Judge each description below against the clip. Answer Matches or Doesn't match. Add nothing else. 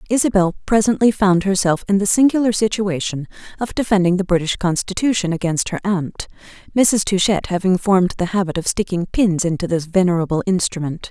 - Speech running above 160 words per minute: Doesn't match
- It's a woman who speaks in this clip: Matches